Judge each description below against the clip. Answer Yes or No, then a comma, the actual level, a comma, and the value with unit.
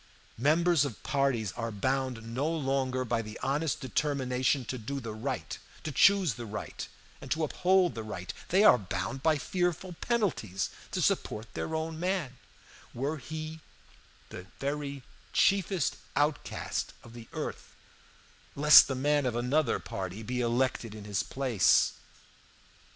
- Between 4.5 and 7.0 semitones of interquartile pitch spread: Yes, average, 5.1 semitones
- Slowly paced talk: No, average, 145 wpm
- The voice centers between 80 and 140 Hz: Yes, low, 135 Hz